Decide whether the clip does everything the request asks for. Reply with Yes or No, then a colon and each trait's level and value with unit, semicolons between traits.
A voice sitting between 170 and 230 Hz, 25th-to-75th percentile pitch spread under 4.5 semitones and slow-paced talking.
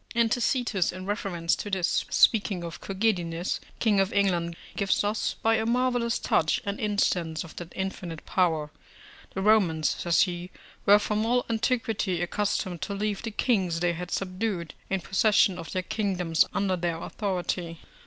No: high, 190 Hz; average, 3.6 semitones; average, 160 wpm